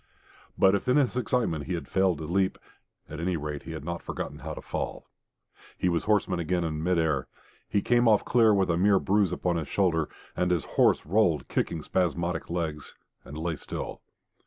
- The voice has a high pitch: No, very low, 90 Hz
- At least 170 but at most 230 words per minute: Yes, average, 200 wpm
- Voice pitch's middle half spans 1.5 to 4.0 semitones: Yes, average, 3.3 semitones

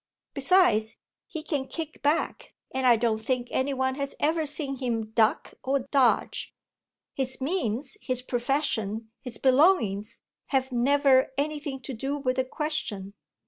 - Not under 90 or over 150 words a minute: Yes, average, 140 wpm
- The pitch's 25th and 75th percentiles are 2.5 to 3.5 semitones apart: Yes, average, 3.2 semitones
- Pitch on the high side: Yes, very high, 265 Hz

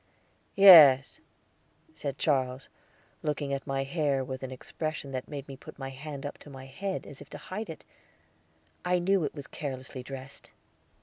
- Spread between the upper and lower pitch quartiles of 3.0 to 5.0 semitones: No, narrow, 2.6 semitones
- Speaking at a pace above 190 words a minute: No, average, 170 wpm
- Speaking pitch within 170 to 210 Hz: No, medium, 140 Hz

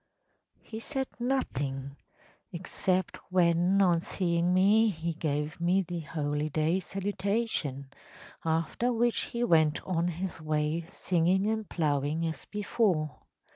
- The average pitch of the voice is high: No, medium, 170 Hz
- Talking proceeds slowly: Yes, slow, 120 wpm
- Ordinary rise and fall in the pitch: Yes, average, 4.1 semitones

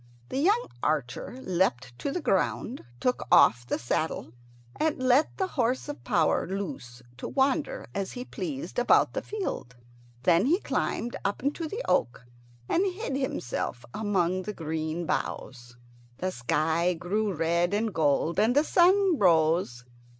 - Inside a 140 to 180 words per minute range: Yes, average, 150 wpm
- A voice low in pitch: No, high, 190 Hz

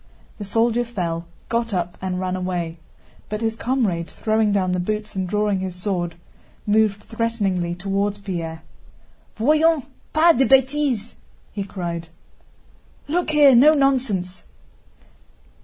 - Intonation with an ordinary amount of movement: Yes, average, 4.7 semitones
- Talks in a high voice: Yes, high, 205 Hz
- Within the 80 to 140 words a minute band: Yes, slow, 135 wpm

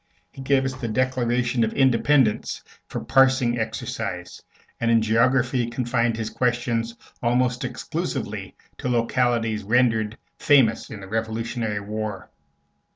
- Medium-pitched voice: No, low, 120 Hz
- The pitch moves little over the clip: Yes, narrow, 2.2 semitones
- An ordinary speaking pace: No, slow, 125 wpm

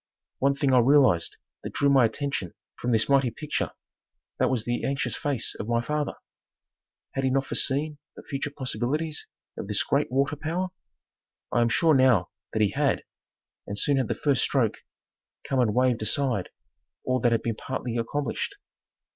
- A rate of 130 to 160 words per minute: No, average, 170 wpm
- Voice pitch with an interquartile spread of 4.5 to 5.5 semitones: No, average, 3.3 semitones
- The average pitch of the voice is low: Yes, low, 130 Hz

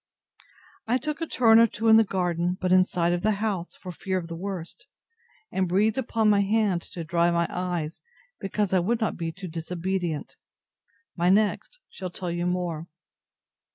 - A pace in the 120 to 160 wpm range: No, average, 185 wpm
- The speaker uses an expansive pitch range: No, average, 3.5 semitones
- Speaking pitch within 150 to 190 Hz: Yes, medium, 185 Hz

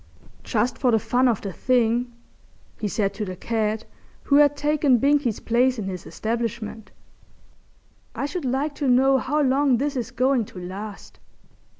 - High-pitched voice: Yes, high, 245 Hz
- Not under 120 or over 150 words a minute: No, average, 165 wpm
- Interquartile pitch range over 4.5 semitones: No, average, 4.0 semitones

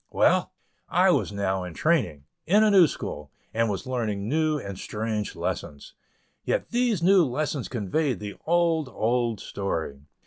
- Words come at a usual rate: Yes, average, 150 wpm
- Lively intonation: Yes, wide, 8.2 semitones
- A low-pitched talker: Yes, low, 120 Hz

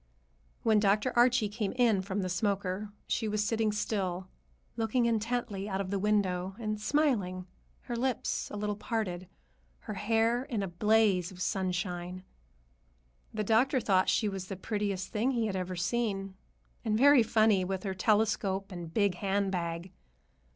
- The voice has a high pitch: Yes, high, 205 Hz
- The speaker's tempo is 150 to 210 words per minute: Yes, average, 155 wpm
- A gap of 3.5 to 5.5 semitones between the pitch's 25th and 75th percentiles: No, average, 3.0 semitones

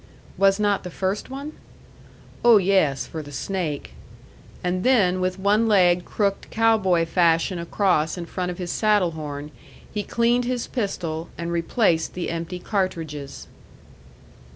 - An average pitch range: Yes, average, 3.6 semitones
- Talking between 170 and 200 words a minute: No, average, 145 wpm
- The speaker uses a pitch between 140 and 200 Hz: Yes, medium, 185 Hz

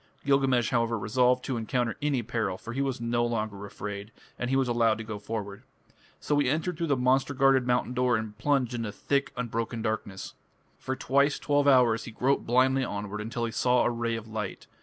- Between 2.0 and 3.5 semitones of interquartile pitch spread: Yes, average, 3.1 semitones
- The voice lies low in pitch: Yes, low, 120 Hz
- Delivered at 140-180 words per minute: No, average, 200 wpm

